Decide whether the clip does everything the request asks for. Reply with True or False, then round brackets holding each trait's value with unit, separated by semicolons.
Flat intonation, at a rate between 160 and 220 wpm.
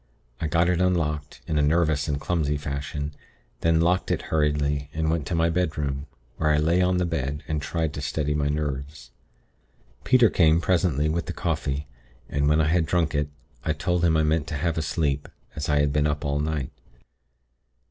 True (2.3 semitones; 200 wpm)